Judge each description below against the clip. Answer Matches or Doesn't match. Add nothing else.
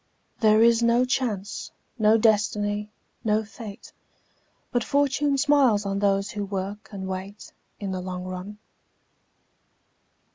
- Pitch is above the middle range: Matches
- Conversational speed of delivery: Doesn't match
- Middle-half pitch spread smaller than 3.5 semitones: Matches